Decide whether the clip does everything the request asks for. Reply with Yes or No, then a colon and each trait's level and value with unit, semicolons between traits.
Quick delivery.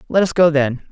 Yes: fast, 260 wpm